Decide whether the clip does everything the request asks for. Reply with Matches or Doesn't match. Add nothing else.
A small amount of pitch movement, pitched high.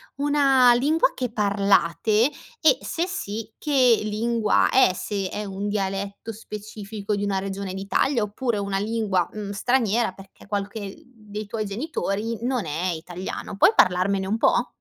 Doesn't match